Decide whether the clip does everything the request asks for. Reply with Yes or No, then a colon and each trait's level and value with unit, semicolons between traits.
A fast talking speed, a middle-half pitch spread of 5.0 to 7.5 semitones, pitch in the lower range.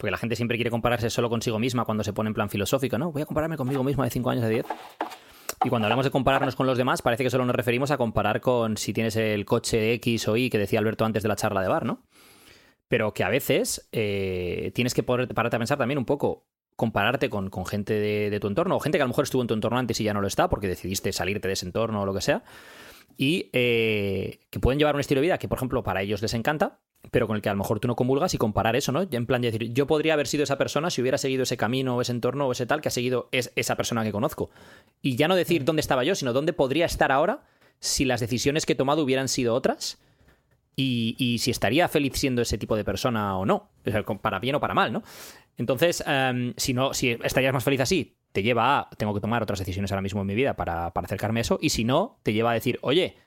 No: fast, 275 wpm; average, 3.8 semitones; low, 120 Hz